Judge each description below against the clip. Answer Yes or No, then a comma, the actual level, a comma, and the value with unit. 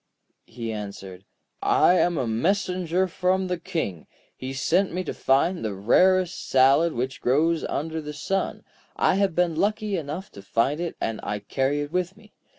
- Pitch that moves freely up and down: Yes, wide, 6.1 semitones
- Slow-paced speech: No, average, 170 wpm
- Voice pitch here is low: No, medium, 160 Hz